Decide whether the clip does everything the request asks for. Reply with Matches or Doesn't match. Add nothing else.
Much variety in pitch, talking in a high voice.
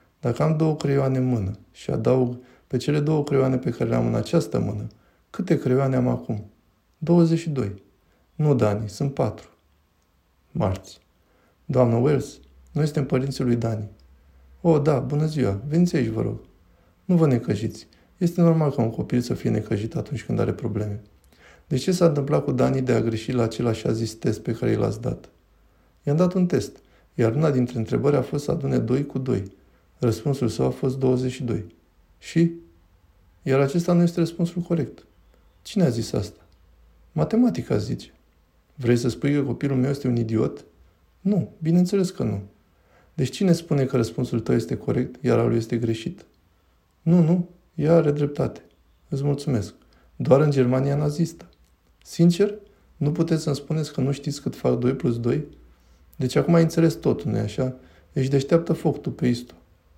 Doesn't match